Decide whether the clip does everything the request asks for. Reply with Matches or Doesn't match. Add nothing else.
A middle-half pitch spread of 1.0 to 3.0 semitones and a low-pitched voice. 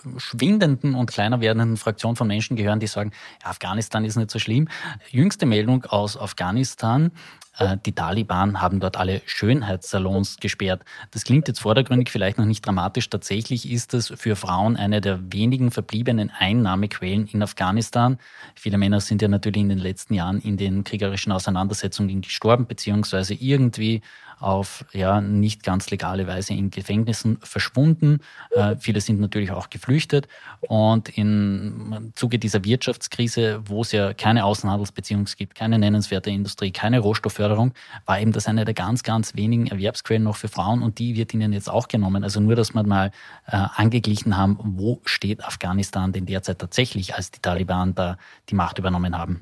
Matches